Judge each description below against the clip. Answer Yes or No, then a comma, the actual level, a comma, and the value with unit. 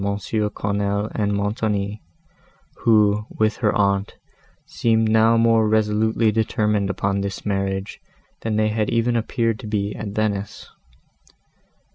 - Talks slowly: Yes, slow, 120 wpm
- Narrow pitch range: Yes, narrow, 1.6 semitones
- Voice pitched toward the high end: No, low, 105 Hz